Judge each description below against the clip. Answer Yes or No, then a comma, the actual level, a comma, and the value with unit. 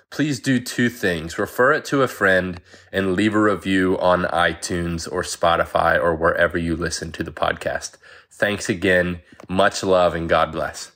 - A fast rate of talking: No, average, 170 wpm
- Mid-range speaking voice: No, very low, 90 Hz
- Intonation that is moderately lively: Yes, average, 3.1 semitones